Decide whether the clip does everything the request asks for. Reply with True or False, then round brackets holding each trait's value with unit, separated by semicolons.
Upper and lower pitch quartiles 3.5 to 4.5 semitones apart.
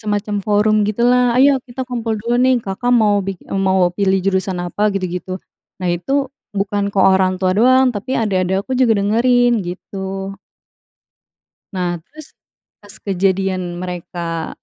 True (3.8 semitones)